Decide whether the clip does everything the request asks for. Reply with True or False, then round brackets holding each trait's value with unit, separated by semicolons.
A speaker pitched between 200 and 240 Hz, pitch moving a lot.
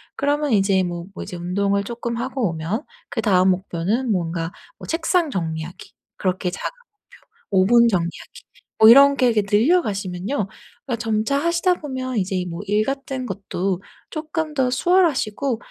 True (215 Hz; 6.7 semitones)